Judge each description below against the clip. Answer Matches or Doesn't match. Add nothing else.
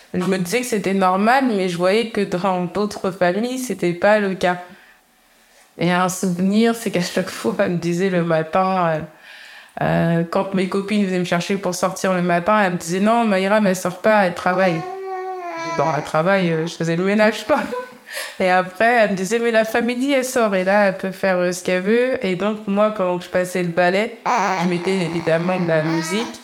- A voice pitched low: Doesn't match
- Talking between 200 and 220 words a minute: Matches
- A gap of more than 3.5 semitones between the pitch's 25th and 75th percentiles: Doesn't match